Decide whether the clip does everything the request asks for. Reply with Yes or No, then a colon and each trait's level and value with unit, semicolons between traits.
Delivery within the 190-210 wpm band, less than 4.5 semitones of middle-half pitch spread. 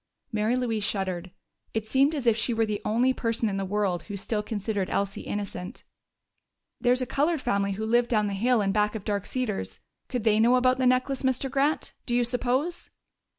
Yes: average, 200 wpm; average, 3.6 semitones